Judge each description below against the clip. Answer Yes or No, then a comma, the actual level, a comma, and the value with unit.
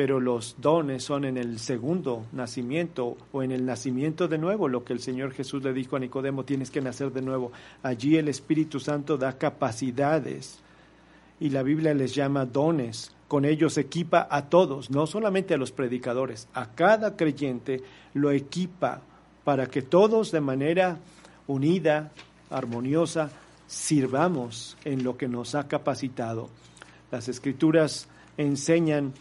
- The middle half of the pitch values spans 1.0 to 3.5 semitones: Yes, average, 3.2 semitones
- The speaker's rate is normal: Yes, average, 150 wpm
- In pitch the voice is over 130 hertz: Yes, medium, 140 Hz